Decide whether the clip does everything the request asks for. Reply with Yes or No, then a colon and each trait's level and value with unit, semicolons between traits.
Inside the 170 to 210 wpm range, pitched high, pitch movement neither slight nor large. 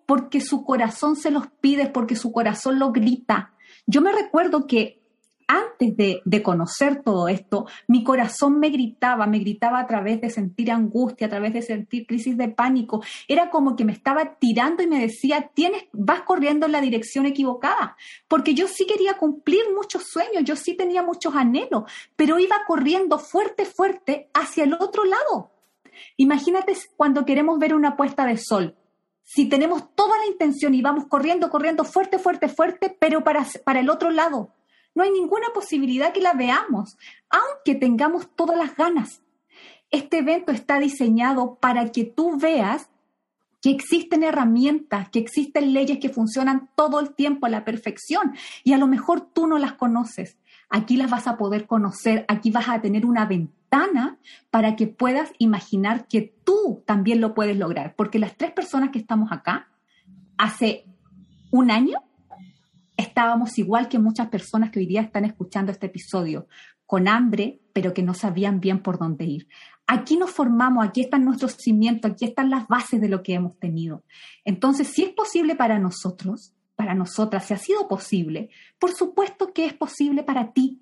No: average, 175 wpm; very high, 260 Hz; wide, 6.0 semitones